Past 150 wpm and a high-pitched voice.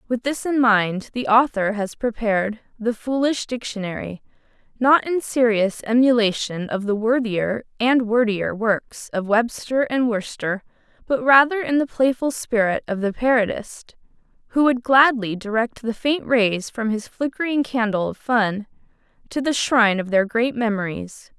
No: average, 145 wpm; high, 230 Hz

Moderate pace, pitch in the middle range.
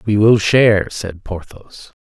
No: average, 150 wpm; low, 100 Hz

